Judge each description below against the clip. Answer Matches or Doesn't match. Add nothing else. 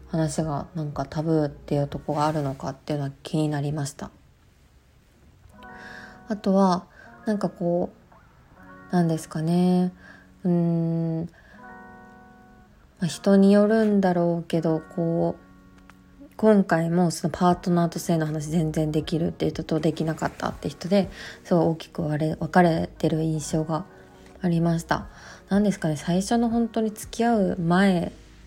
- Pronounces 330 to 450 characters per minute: Doesn't match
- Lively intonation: Doesn't match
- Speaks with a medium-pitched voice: Matches